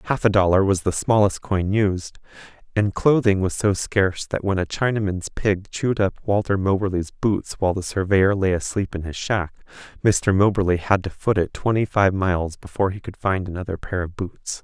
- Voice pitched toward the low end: Yes, very low, 95 Hz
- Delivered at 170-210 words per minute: Yes, average, 195 wpm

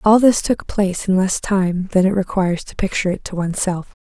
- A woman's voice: Yes, female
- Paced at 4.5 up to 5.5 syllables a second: No, 5.8 syllables/s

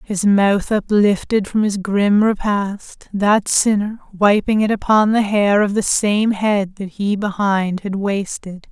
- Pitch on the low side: No, high, 205 Hz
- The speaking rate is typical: Yes, average, 160 wpm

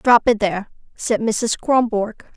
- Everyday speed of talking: Yes, average, 155 wpm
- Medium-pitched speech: No, high, 225 Hz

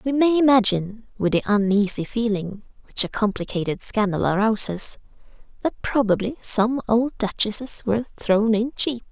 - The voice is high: Yes, high, 220 Hz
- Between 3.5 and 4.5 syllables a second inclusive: No, 4.9 syllables/s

